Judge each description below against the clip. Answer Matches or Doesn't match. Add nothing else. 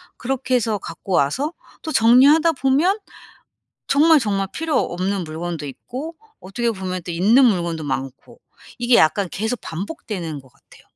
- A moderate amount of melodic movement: Doesn't match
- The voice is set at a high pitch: Matches